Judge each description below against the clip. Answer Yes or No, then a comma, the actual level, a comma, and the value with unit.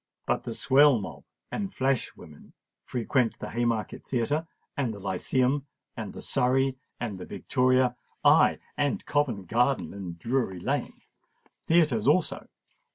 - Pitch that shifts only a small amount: No, average, 3.7 semitones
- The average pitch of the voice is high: No, low, 125 Hz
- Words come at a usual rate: No, slow, 115 wpm